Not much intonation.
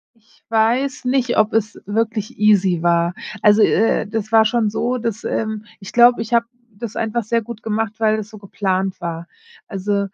Yes: narrow, 2.3 semitones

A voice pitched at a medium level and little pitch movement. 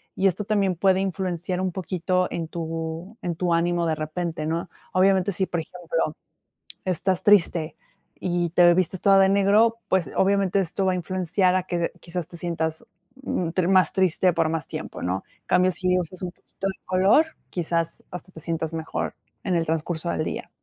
Yes: medium, 180 Hz; narrow, 2.2 semitones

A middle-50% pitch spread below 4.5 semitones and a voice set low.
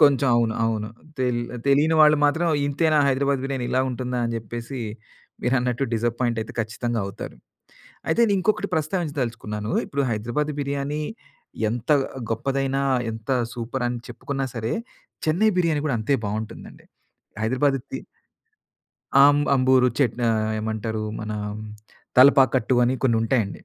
Yes: average, 3.6 semitones; low, 130 Hz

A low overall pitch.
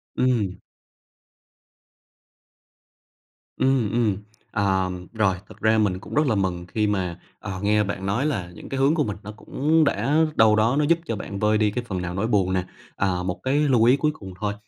Yes: low, 105 Hz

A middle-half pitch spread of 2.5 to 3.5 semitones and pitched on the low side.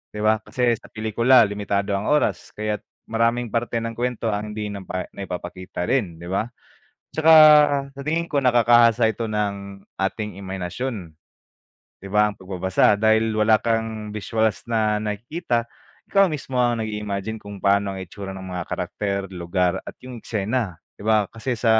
Yes: average, 3.0 semitones; low, 110 Hz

